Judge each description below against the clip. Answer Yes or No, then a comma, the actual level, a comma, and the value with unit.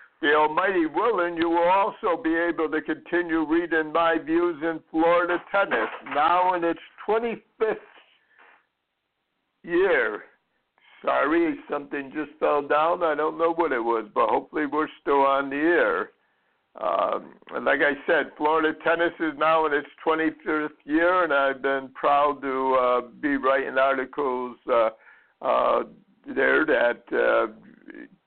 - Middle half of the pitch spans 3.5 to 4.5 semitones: No, average, 3.1 semitones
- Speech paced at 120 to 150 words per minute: Yes, average, 140 wpm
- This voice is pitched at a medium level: Yes, medium, 160 Hz